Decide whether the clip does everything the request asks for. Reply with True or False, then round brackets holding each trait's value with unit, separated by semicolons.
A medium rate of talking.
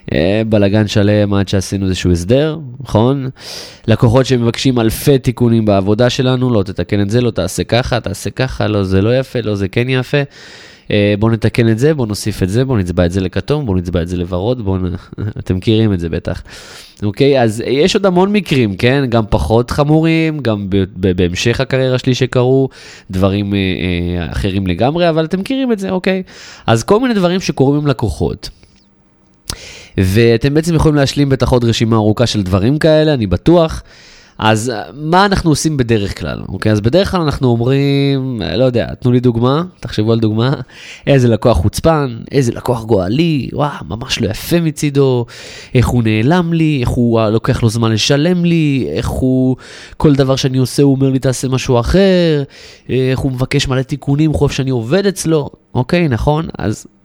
False (180 wpm)